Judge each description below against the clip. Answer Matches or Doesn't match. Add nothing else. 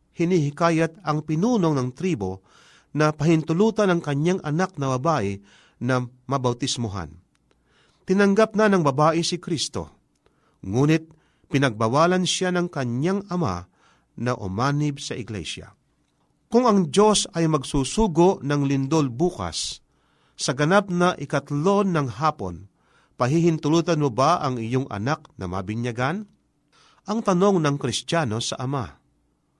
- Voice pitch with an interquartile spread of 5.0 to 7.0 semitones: Matches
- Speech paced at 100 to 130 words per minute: Matches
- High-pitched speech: Doesn't match